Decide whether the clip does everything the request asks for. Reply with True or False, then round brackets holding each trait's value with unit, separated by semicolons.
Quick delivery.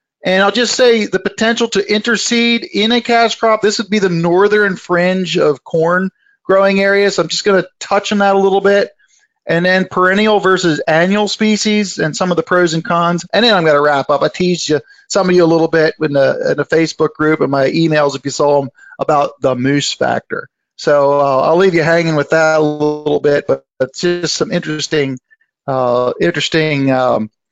True (215 wpm)